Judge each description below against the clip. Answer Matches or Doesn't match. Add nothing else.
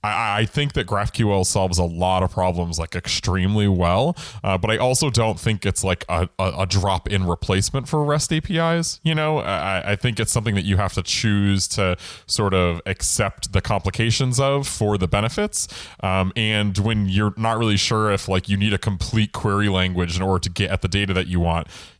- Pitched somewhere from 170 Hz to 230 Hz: Doesn't match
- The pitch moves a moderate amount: Matches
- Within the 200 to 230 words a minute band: Matches